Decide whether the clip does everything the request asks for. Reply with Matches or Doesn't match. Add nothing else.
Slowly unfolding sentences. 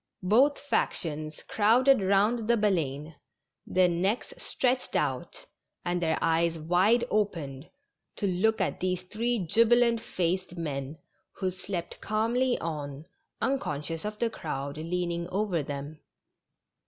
Matches